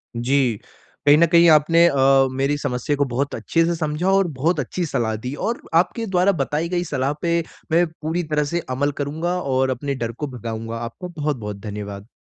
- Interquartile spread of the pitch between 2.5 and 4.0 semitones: No, average, 4.9 semitones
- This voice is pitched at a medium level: Yes, medium, 145 Hz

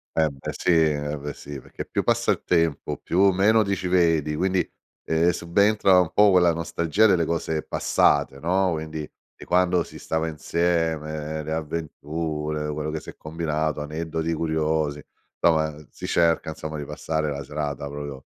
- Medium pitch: No, very low, 80 Hz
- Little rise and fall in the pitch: Yes, narrow, 2.0 semitones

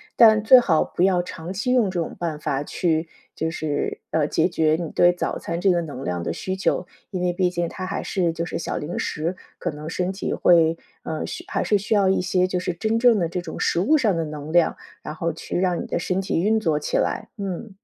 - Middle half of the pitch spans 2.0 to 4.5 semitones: Yes, average, 3.0 semitones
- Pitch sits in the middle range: Yes, medium, 175 Hz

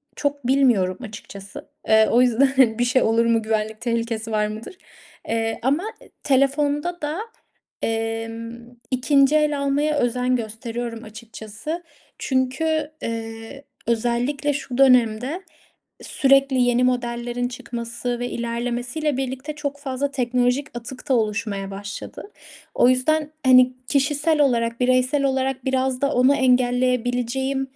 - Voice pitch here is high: Yes, very high, 250 Hz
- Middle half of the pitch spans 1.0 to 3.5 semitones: Yes, average, 3.0 semitones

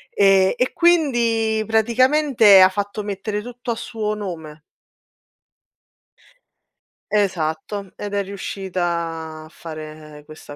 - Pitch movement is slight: No, average, 5.0 semitones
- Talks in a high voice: Yes, high, 200 Hz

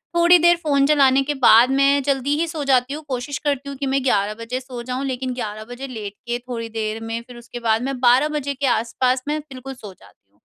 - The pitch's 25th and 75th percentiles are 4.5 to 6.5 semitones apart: No, average, 2.7 semitones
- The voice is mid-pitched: No, very high, 260 Hz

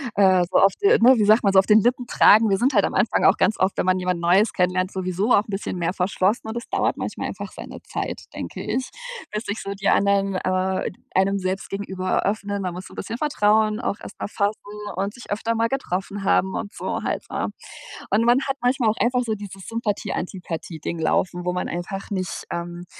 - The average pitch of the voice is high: Yes, high, 200 Hz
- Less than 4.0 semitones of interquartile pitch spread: Yes, average, 2.9 semitones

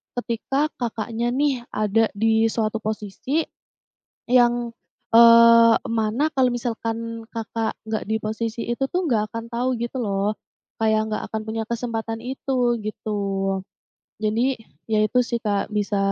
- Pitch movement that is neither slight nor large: No, narrow, 1.8 semitones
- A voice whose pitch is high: Yes, high, 230 Hz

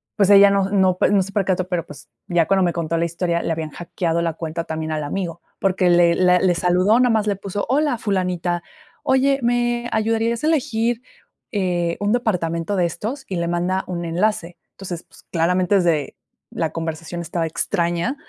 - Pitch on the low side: No, medium, 180 Hz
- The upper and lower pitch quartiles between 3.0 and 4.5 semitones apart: Yes, average, 3.3 semitones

